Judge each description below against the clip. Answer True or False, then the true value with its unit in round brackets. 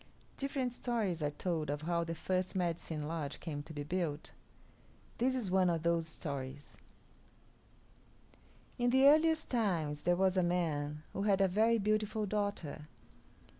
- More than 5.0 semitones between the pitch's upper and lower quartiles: True (5.5 semitones)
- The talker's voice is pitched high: False (175 Hz)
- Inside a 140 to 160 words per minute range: True (150 wpm)